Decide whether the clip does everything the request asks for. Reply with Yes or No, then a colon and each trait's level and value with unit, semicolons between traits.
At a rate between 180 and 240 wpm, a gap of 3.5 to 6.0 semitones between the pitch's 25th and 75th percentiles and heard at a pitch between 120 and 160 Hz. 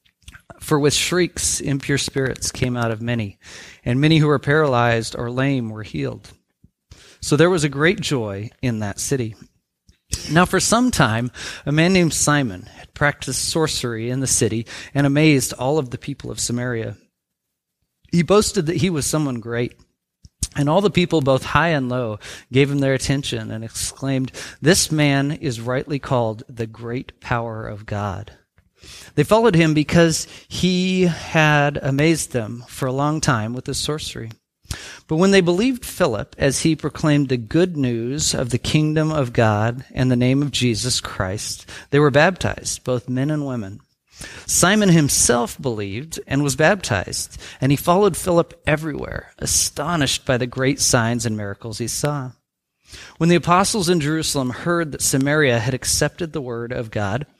No: average, 165 wpm; average, 4.6 semitones; low, 135 Hz